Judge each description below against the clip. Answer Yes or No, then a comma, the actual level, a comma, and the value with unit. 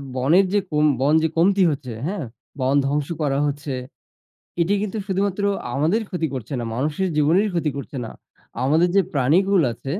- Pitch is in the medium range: Yes, medium, 150 Hz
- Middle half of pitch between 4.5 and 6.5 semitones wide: Yes, wide, 5.5 semitones